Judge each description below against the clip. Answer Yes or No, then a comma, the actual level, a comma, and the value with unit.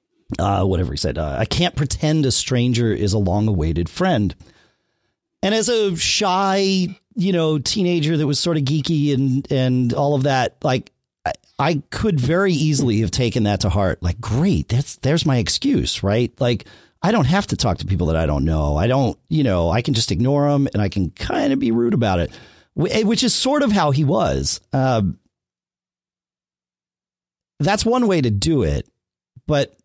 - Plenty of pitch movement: Yes, wide, 7.8 semitones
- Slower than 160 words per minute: No, average, 190 wpm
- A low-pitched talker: Yes, low, 130 Hz